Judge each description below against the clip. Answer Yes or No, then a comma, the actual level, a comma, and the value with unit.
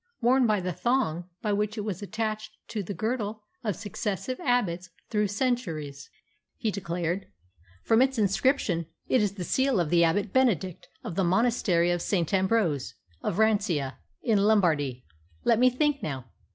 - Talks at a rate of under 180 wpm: Yes, average, 160 wpm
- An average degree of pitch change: Yes, average, 4.7 semitones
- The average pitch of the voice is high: Yes, high, 205 Hz